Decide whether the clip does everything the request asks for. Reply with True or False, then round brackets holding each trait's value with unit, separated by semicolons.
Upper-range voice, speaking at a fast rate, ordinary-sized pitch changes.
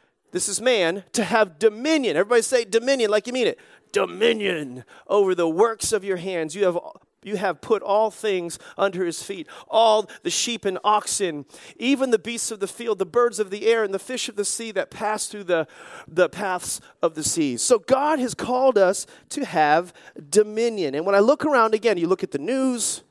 True (210 Hz; 210 wpm; 4.0 semitones)